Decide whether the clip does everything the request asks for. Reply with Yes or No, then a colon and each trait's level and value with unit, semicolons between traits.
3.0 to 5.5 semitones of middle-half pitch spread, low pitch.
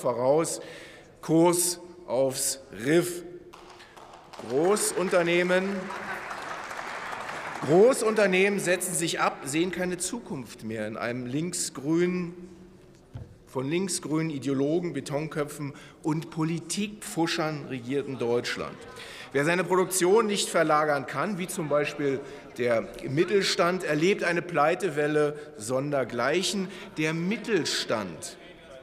No: average, 4.0 semitones; medium, 170 Hz